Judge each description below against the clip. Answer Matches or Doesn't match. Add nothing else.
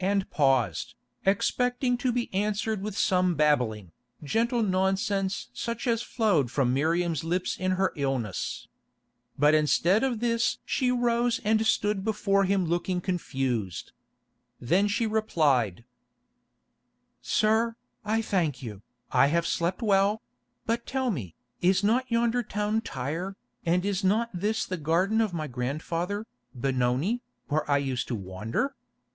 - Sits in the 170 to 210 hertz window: Matches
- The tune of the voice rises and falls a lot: Matches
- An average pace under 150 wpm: Matches